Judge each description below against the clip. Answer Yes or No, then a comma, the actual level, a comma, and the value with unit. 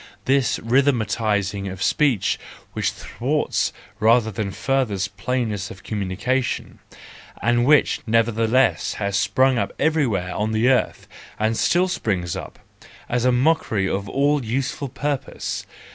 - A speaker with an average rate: No, slow, 125 wpm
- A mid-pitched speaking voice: No, low, 115 Hz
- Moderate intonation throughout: Yes, average, 4.6 semitones